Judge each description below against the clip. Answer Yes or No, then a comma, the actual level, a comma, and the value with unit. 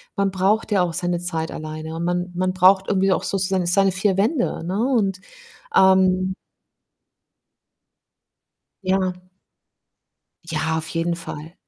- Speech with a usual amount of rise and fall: No, narrow, 2.1 semitones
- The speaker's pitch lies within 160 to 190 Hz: Yes, medium, 185 Hz